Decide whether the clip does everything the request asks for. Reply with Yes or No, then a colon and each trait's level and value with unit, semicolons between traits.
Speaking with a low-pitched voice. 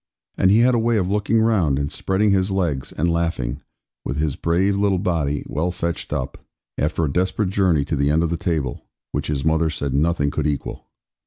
Yes: very low, 85 Hz